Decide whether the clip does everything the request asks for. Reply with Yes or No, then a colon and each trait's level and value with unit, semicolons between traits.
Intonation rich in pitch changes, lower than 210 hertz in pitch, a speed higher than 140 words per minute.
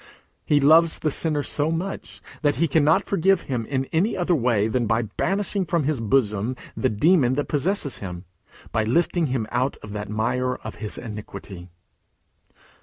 Yes: wide, 6.7 semitones; low, 135 Hz; average, 170 wpm